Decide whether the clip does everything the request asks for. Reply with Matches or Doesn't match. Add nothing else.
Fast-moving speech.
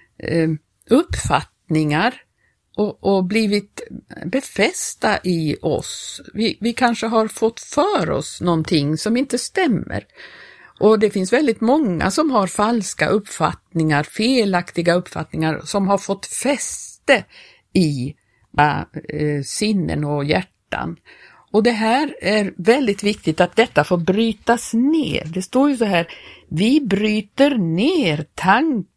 Doesn't match